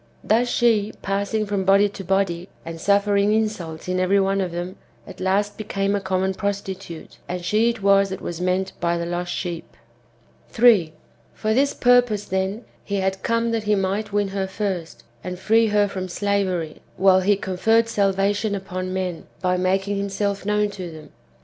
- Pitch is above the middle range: Yes, high, 195 Hz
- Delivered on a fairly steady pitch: Yes, narrow, 2.0 semitones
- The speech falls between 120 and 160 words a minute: No, average, 175 wpm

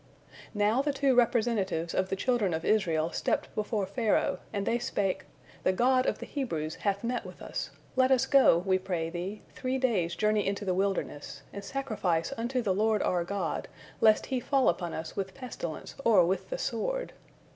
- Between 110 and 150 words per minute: No, average, 185 wpm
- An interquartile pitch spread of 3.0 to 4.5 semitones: No, average, 5.2 semitones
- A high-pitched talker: Yes, high, 205 Hz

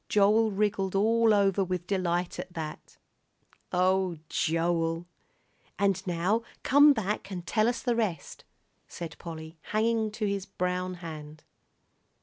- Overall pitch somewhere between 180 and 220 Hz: Yes, high, 190 Hz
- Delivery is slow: Yes, slow, 130 wpm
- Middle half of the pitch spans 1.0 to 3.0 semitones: No, average, 3.5 semitones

